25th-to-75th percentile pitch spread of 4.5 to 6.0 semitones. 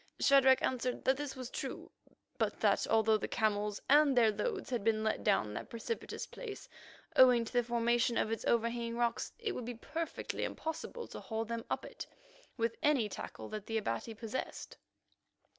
No: average, 3.0 semitones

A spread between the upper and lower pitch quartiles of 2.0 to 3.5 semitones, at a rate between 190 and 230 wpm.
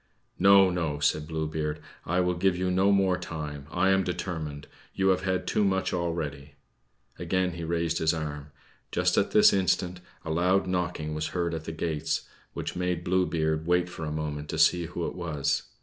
Yes: average, 2.8 semitones; average, 195 wpm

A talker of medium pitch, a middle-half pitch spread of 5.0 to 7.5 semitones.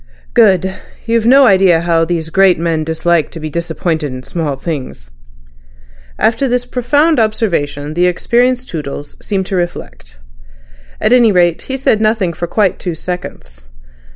Yes: medium, 175 Hz; wide, 5.6 semitones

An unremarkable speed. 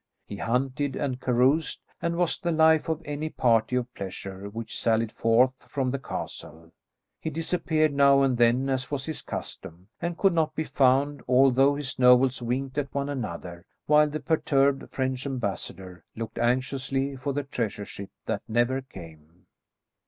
Yes: average, 160 wpm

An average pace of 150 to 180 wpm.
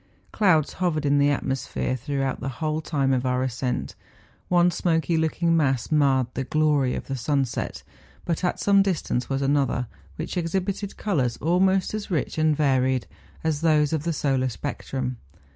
Yes: average, 160 wpm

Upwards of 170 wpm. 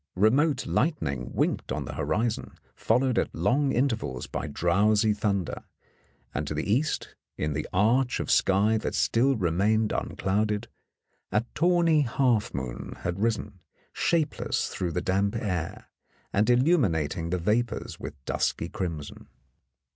No: average, 140 wpm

